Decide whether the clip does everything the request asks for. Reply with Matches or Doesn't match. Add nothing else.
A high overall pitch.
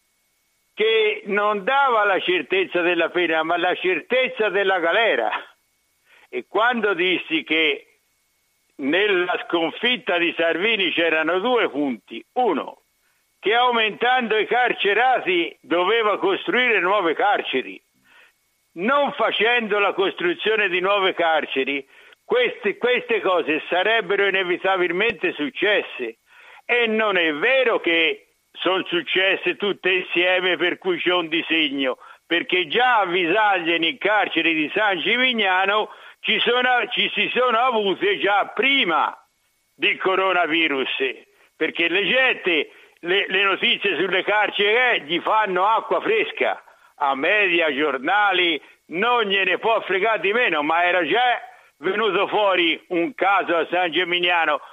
Matches